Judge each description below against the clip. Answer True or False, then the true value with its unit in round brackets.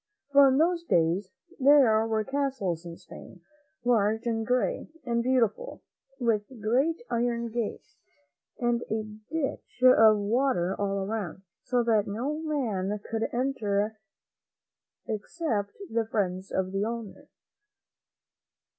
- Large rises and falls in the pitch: False (4.0 semitones)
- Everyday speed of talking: False (120 wpm)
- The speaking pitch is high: True (225 Hz)